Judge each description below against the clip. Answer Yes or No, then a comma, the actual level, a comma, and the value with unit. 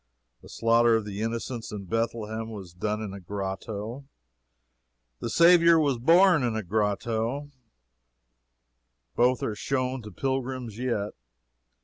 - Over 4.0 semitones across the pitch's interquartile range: No, average, 3.4 semitones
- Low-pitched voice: Yes, low, 115 Hz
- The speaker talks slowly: Yes, slow, 125 wpm